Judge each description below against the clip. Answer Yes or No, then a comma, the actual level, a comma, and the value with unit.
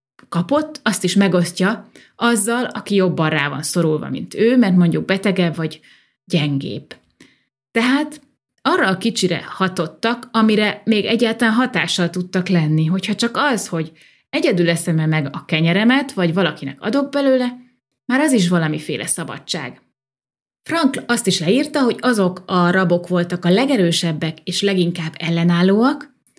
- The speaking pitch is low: No, medium, 185 Hz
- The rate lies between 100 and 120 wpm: No, average, 135 wpm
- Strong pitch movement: Yes, wide, 5.7 semitones